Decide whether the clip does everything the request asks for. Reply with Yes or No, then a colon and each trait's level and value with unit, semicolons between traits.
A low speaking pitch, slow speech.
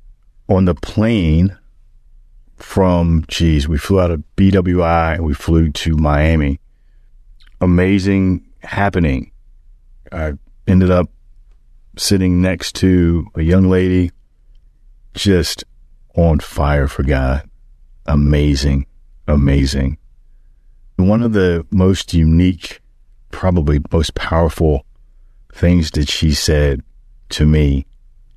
Yes: very low, 80 Hz; slow, 95 wpm